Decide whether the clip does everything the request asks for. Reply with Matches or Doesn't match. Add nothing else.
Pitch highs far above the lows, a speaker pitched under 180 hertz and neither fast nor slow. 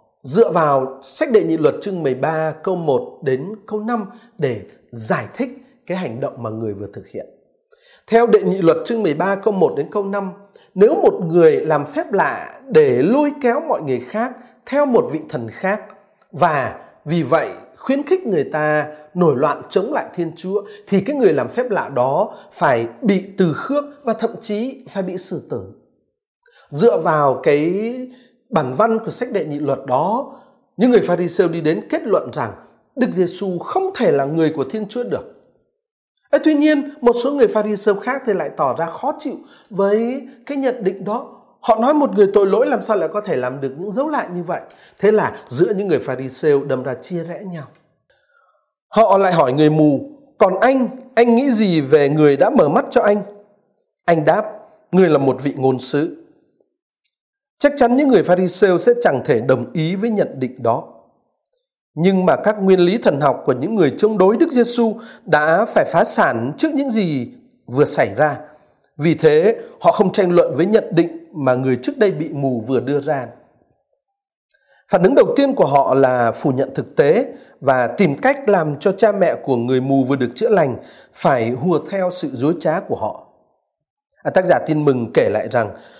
Doesn't match